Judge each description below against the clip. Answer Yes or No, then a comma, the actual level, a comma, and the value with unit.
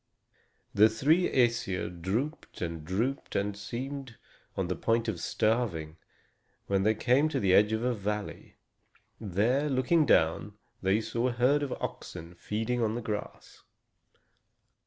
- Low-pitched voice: Yes, low, 110 Hz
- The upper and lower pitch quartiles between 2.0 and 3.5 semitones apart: No, average, 4.3 semitones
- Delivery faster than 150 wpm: No, average, 140 wpm